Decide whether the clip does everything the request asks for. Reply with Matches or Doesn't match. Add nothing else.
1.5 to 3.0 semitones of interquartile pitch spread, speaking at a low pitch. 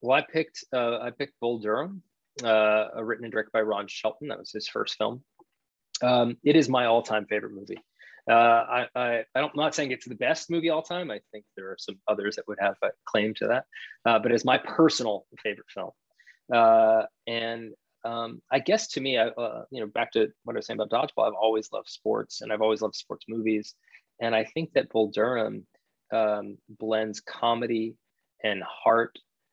Matches